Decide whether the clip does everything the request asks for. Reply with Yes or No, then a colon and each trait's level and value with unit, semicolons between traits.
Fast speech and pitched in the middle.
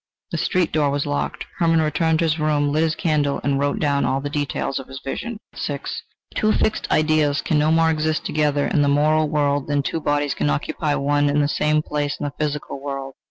Yes: fast, 220 wpm; medium, 145 Hz